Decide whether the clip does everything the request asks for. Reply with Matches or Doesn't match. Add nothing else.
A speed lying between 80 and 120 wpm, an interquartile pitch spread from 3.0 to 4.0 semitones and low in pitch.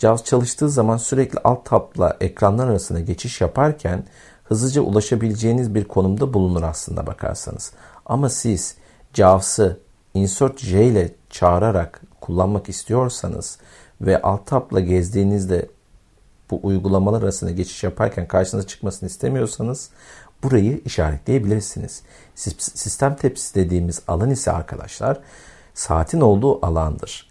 Doesn't match